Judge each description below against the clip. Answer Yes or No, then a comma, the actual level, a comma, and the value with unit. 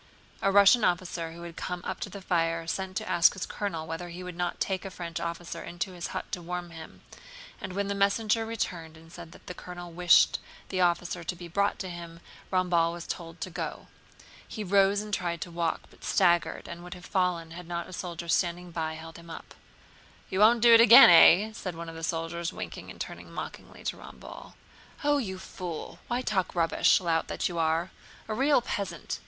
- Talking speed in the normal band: No, fast, 210 wpm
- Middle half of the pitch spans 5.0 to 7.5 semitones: No, narrow, 2.4 semitones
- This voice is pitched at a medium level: Yes, medium, 175 Hz